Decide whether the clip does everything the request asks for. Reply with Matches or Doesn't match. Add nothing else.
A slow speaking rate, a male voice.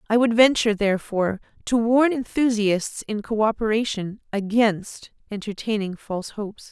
Doesn't match